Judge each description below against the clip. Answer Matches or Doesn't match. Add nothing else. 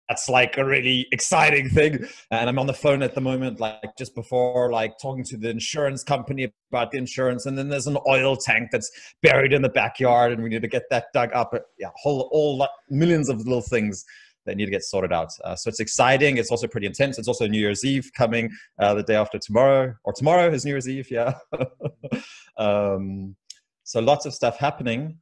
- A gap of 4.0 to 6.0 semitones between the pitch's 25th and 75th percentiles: Doesn't match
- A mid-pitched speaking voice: Doesn't match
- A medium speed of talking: Doesn't match